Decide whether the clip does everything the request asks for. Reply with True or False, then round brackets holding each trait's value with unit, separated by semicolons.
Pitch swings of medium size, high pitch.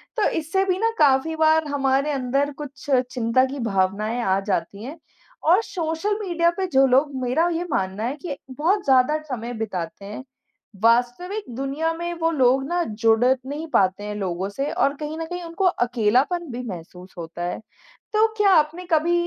False (6.1 semitones; 275 Hz)